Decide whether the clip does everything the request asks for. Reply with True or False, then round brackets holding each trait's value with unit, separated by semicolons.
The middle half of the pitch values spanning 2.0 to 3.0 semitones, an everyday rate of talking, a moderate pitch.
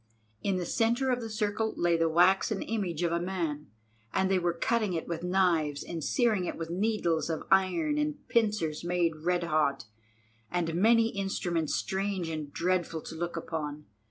False (3.9 semitones; 175 wpm; 175 Hz)